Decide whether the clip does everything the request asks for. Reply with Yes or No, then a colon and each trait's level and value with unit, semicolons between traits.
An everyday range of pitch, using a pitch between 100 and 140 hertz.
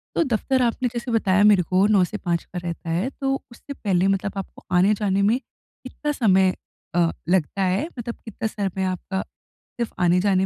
No: average, 3.7 semitones; high, 195 Hz